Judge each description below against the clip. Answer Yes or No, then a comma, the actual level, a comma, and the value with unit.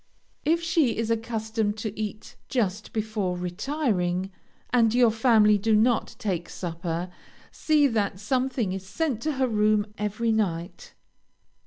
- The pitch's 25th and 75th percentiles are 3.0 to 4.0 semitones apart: Yes, average, 3.6 semitones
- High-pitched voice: Yes, high, 215 Hz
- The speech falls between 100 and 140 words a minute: Yes, slow, 135 wpm